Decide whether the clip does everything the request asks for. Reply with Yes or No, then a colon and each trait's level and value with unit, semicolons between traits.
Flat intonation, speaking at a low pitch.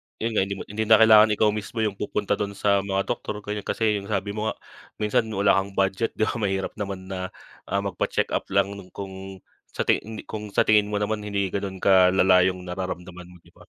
Yes: narrow, 1.6 semitones; low, 100 Hz